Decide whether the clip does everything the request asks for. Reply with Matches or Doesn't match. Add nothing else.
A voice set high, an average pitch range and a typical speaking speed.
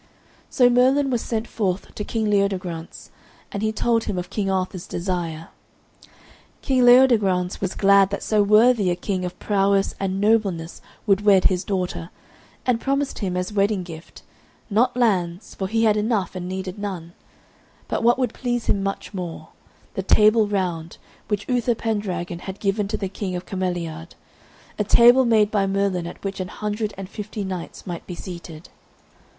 Matches